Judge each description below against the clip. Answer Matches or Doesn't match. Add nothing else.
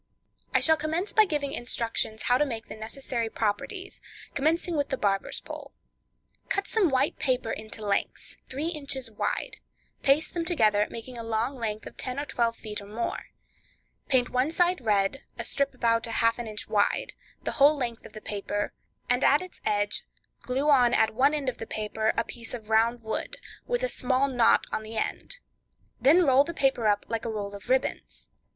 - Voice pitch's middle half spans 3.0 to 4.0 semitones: Doesn't match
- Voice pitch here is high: Matches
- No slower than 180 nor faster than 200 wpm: Matches